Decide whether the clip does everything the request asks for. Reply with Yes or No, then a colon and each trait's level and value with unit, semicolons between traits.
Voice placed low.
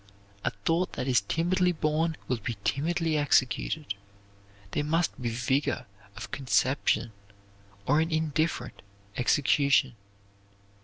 No: medium, 145 Hz